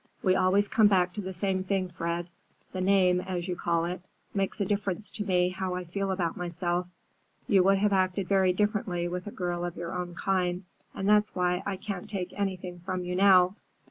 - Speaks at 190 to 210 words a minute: Yes, fast, 205 wpm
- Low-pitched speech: No, medium, 185 Hz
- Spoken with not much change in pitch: Yes, narrow, 1.7 semitones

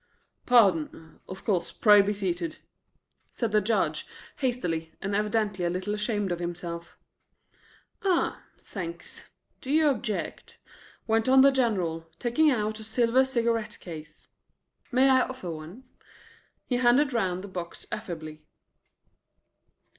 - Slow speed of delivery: Yes, slow, 125 wpm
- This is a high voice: Yes, high, 210 Hz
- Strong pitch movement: Yes, wide, 5.7 semitones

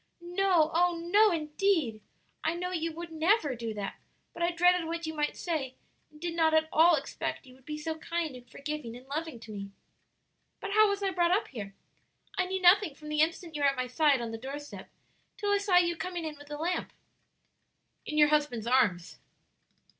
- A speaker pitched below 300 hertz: No, very high, 315 Hz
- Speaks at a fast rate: Yes, fast, 210 wpm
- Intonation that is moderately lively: Yes, average, 4.0 semitones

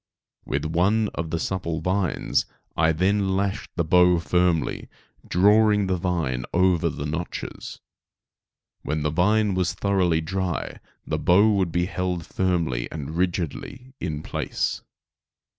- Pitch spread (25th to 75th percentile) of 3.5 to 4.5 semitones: No, average, 3.0 semitones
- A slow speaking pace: Yes, slow, 130 wpm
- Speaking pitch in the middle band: No, very low, 90 Hz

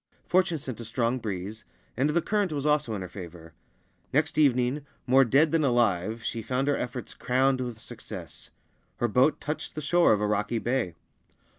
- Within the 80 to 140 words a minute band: No, average, 180 wpm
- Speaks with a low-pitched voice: Yes, low, 125 Hz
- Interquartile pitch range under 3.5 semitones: No, average, 4.8 semitones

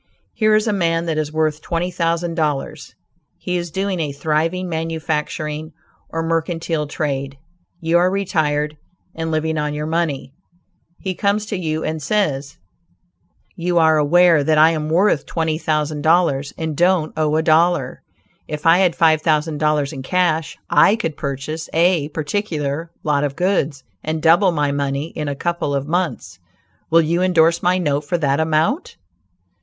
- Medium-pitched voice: Yes, medium, 160 Hz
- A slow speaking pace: No, average, 165 wpm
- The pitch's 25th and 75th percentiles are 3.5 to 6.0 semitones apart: No, narrow, 2.4 semitones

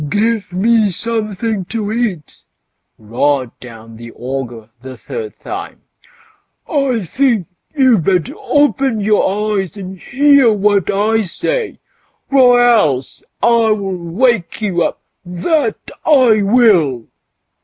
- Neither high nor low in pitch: No, high, 210 Hz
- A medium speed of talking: No, slow, 110 wpm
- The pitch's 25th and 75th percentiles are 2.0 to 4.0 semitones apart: No, wide, 5.6 semitones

